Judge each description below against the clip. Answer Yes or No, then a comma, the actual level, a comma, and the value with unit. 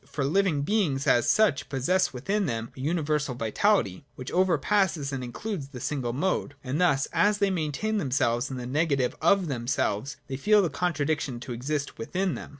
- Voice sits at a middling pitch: Yes, medium, 145 Hz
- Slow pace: No, average, 175 wpm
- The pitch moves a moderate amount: No, wide, 6.2 semitones